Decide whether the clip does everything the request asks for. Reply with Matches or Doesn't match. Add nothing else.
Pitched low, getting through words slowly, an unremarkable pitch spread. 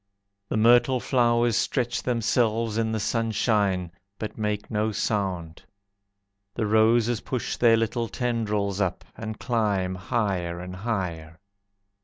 Matches